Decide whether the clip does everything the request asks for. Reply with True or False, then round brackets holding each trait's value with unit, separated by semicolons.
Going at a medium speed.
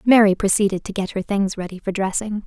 False (220 wpm)